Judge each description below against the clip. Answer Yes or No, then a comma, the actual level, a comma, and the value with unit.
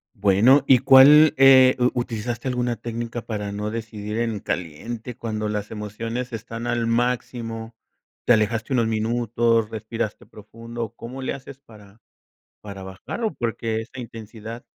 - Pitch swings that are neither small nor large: No, narrow, 2.1 semitones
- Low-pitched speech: Yes, low, 115 Hz